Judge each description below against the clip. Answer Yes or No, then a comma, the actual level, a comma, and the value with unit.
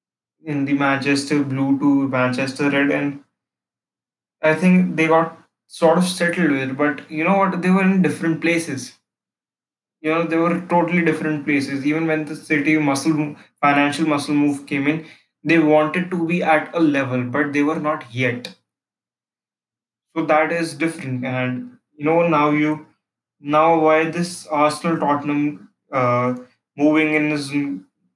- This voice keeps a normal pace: Yes, average, 155 wpm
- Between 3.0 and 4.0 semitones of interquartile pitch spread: No, narrow, 2.4 semitones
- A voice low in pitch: No, medium, 150 Hz